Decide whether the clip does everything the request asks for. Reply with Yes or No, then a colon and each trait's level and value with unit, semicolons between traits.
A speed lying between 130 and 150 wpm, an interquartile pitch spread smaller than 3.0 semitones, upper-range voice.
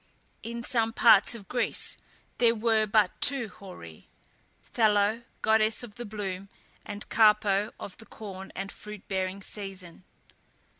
Yes: slow, 135 wpm; narrow, 2.5 semitones; high, 210 Hz